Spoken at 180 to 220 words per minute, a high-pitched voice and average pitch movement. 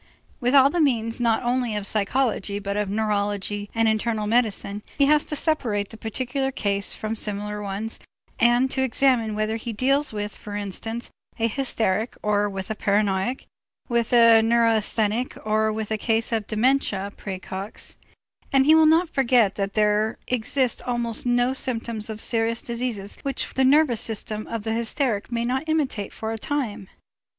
No: average, 165 wpm; high, 225 Hz; average, 3.2 semitones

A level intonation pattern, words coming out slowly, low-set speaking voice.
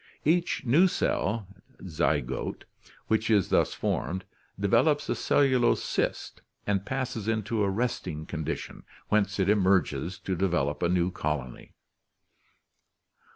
No: average, 4.7 semitones; slow, 120 wpm; low, 100 Hz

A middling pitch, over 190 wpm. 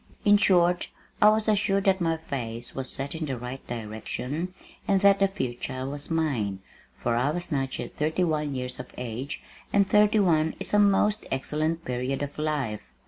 No: medium, 150 Hz; average, 185 wpm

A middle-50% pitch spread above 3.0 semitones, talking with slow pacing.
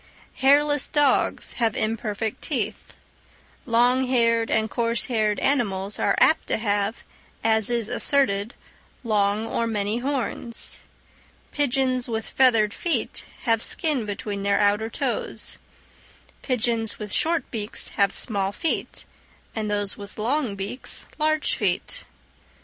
Yes: average, 3.7 semitones; slow, 120 wpm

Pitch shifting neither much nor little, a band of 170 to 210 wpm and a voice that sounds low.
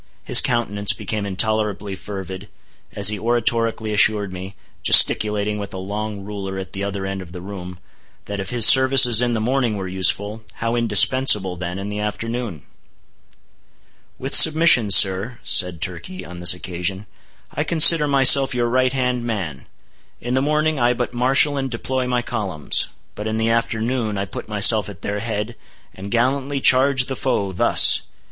No: average, 4.2 semitones; average, 160 wpm; low, 110 Hz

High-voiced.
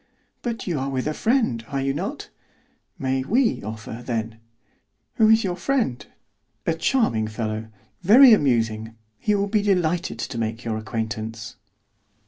No: low, 135 Hz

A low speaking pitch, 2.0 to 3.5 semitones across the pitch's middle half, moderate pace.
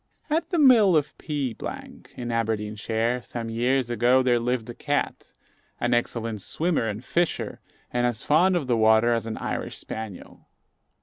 No: low, 120 Hz; average, 4.3 semitones; average, 160 wpm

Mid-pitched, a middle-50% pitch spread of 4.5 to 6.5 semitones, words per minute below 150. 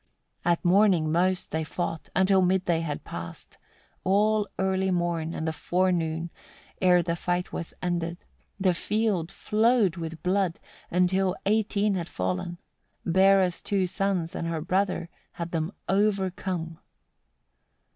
No: medium, 180 Hz; narrow, 2.5 semitones; slow, 135 wpm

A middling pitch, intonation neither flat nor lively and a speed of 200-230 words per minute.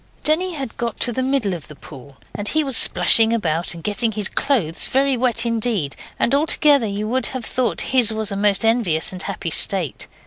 No: high, 225 Hz; average, 4.8 semitones; fast, 205 wpm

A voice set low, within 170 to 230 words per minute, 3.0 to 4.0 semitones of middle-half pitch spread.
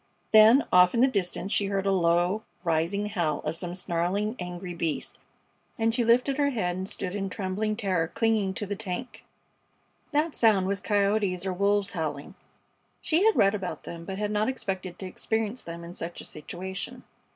No: high, 195 Hz; average, 185 wpm; average, 3.5 semitones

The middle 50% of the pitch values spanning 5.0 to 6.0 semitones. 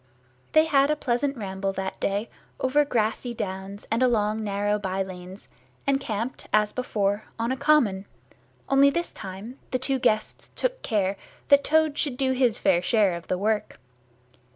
Yes: wide, 5.4 semitones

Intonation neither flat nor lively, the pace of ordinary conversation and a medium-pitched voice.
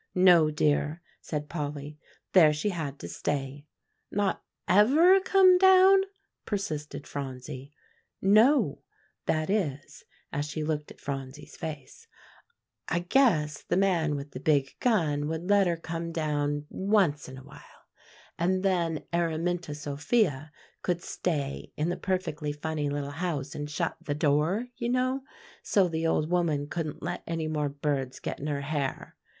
Yes: average, 4.1 semitones; average, 145 wpm; medium, 155 Hz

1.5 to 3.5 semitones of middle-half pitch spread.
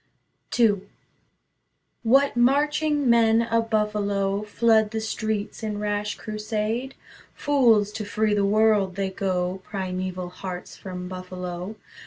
Yes: average, 2.8 semitones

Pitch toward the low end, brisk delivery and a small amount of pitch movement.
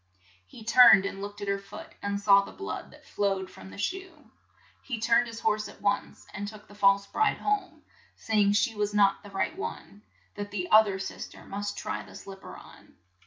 No: high, 205 Hz; fast, 215 wpm; narrow, 2.2 semitones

